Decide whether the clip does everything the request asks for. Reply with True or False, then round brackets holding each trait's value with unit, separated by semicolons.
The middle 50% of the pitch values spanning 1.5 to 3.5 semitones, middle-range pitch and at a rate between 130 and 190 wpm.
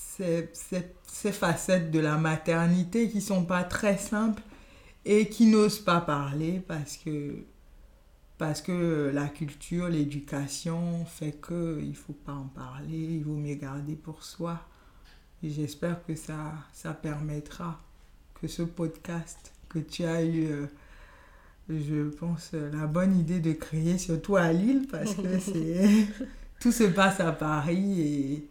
True (3.2 semitones; 165 Hz; 145 wpm)